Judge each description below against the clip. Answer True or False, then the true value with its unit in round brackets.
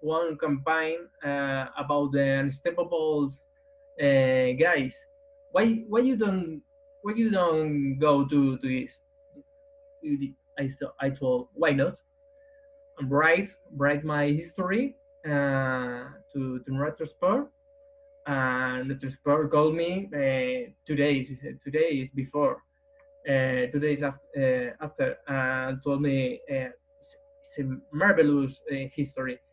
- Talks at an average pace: False (120 wpm)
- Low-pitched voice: False (150 Hz)